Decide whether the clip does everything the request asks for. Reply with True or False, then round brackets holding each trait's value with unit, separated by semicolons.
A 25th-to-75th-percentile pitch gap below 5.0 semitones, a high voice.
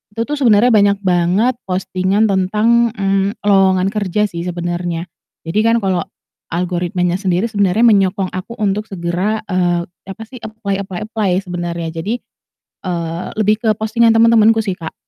True (3.5 semitones; 195 Hz)